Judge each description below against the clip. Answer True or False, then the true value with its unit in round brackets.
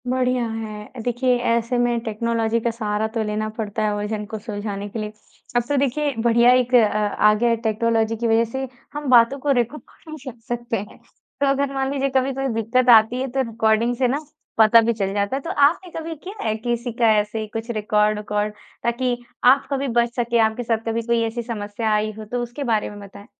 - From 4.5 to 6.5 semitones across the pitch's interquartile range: False (2.7 semitones)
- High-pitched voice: True (230 Hz)